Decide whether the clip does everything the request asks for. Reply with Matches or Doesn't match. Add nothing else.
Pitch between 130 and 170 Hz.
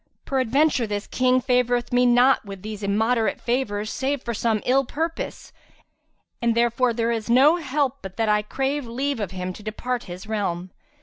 Doesn't match